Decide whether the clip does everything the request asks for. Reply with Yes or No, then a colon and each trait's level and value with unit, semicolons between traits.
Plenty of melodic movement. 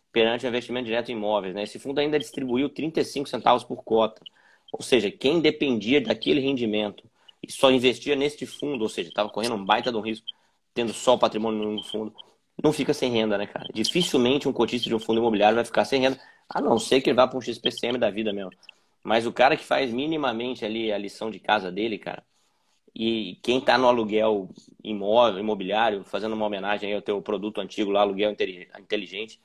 No: average, 2.8 semitones